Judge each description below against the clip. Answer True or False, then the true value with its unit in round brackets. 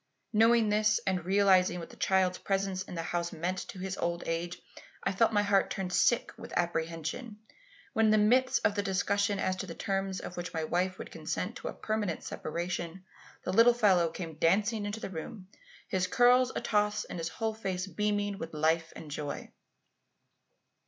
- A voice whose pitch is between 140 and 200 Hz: True (190 Hz)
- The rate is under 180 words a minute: False (185 wpm)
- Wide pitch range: False (3.2 semitones)